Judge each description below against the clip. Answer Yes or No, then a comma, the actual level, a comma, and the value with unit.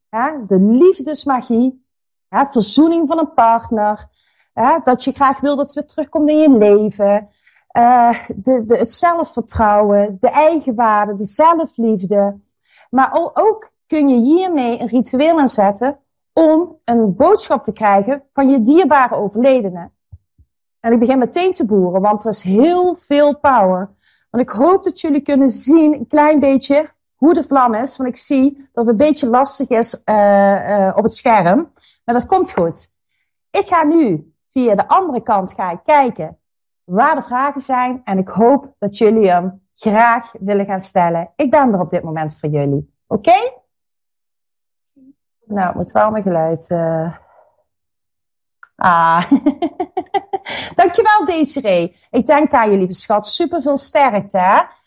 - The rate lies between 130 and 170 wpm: Yes, average, 155 wpm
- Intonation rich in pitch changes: Yes, wide, 6.4 semitones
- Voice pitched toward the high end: Yes, very high, 250 Hz